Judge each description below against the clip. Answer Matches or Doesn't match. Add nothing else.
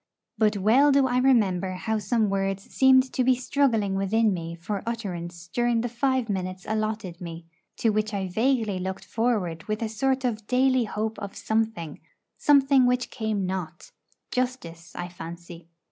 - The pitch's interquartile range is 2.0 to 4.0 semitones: Doesn't match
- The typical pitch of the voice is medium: Doesn't match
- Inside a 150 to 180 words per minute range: Matches